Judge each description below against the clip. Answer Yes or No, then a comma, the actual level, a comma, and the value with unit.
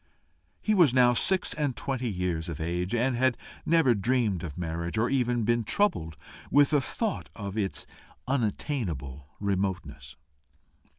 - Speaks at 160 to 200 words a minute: No, average, 140 wpm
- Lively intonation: Yes, wide, 6.9 semitones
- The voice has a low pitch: Yes, low, 110 Hz